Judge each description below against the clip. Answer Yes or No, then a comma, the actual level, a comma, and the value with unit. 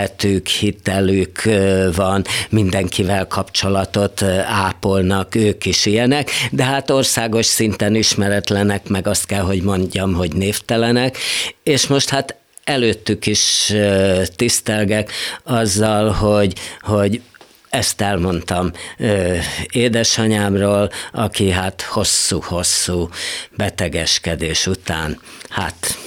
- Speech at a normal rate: No, slow, 85 wpm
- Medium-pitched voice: No, low, 100 Hz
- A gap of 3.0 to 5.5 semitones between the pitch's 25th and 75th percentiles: No, narrow, 2.6 semitones